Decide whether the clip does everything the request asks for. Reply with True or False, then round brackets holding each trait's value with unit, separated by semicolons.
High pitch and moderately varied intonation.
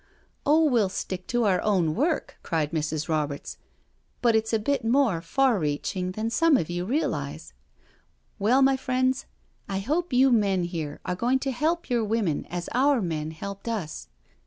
False (210 Hz; 7.3 semitones)